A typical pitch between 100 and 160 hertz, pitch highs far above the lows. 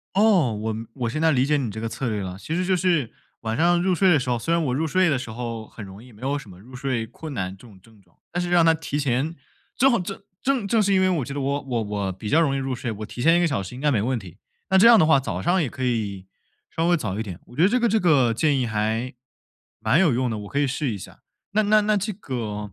Yes: low, 135 Hz; wide, 7.3 semitones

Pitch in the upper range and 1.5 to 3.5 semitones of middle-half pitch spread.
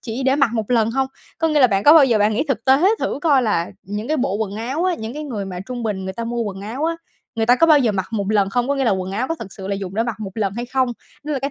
No: high, 230 Hz; average, 4.8 semitones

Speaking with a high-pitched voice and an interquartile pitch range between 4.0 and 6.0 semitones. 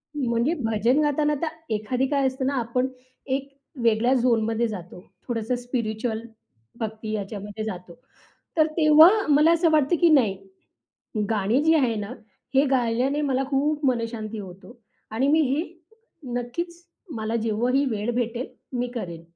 Yes: high, 245 Hz; average, 4.3 semitones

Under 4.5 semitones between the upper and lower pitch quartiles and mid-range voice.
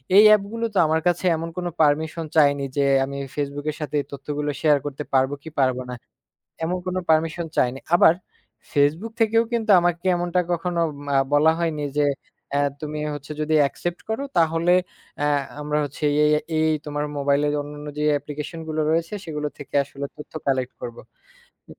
Yes: average, 2.7 semitones; medium, 150 Hz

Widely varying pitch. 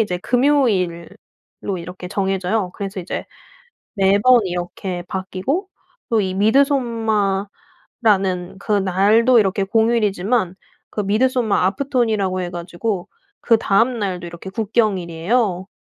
No: average, 3.6 semitones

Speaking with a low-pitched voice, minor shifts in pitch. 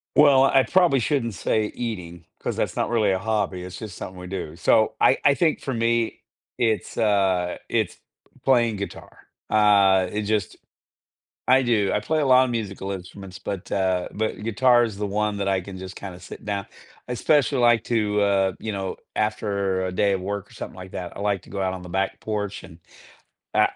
No: low, 105 Hz; average, 3.3 semitones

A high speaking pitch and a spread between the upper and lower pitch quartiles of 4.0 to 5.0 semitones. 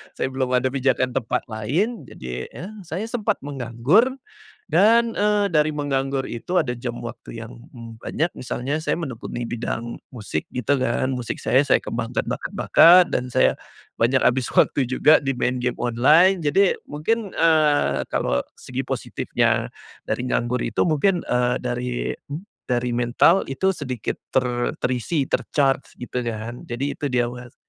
No: low, 130 Hz; average, 4.3 semitones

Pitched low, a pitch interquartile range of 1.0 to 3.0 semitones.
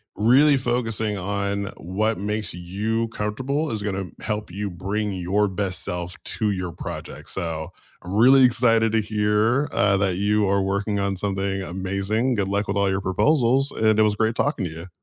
Yes: low, 105 Hz; narrow, 2.6 semitones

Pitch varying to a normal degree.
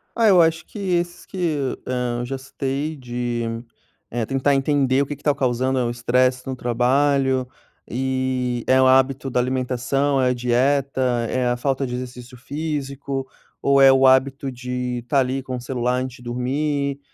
No: narrow, 1.8 semitones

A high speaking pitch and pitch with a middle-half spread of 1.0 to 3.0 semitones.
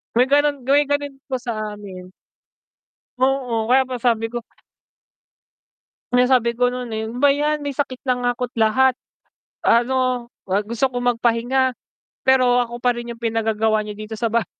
Yes: high, 245 Hz; narrow, 2.5 semitones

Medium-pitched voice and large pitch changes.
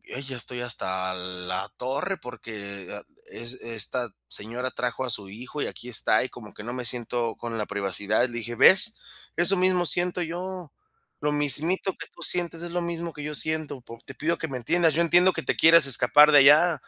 No: low, 130 Hz; wide, 6.4 semitones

